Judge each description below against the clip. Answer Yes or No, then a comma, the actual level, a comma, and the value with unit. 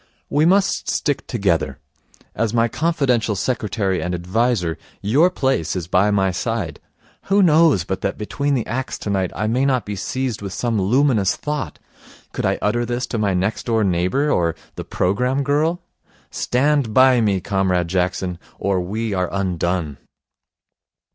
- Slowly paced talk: No, average, 155 wpm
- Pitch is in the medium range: No, low, 110 Hz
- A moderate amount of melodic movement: No, wide, 6.0 semitones